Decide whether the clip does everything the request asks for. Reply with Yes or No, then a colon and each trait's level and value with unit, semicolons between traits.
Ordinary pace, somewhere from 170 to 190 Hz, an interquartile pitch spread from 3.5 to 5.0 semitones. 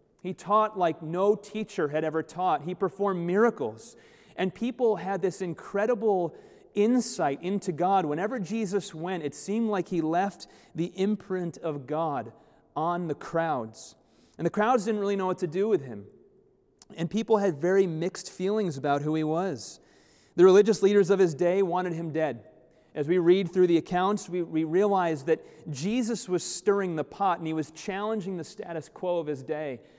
Yes: average, 180 wpm; medium, 185 Hz; average, 3.9 semitones